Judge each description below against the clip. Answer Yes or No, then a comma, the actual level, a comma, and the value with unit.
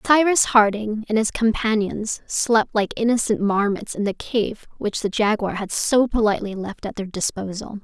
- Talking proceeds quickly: No, average, 170 wpm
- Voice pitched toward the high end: Yes, high, 215 Hz